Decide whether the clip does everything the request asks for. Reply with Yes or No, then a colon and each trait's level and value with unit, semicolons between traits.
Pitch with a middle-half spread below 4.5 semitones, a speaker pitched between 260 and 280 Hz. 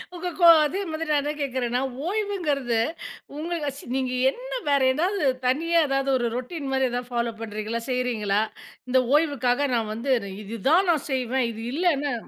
No: average, 4.8 semitones; very high, 275 Hz